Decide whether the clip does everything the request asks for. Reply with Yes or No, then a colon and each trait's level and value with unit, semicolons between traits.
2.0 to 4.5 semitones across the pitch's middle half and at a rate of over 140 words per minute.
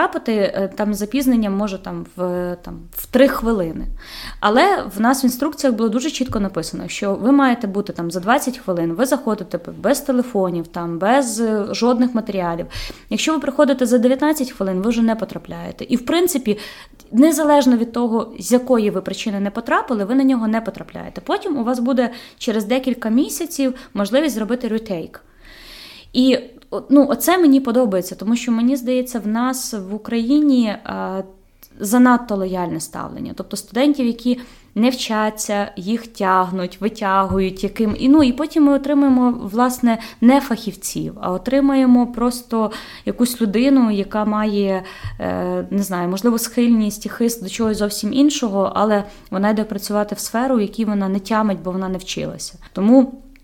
Yes: average, 4.2 semitones; fast, 155 wpm